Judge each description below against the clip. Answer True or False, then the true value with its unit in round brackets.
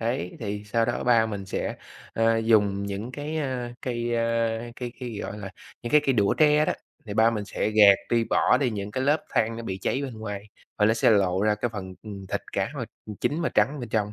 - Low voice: True (115 Hz)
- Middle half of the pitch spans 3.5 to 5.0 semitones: False (2.9 semitones)